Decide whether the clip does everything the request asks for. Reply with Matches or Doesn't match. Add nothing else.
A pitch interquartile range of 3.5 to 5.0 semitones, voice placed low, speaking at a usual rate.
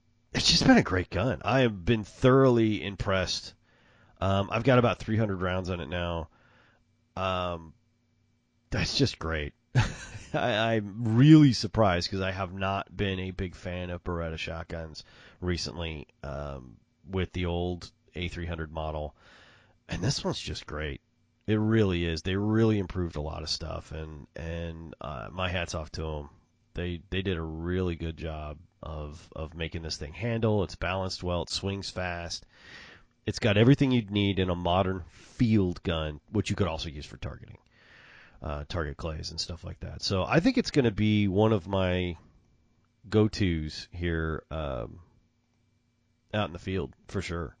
Matches